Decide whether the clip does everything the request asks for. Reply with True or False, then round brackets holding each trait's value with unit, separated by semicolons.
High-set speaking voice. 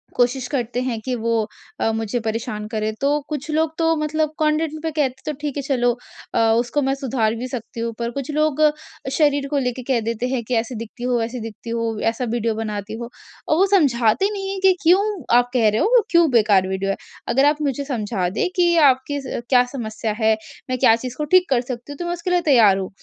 True (250 Hz)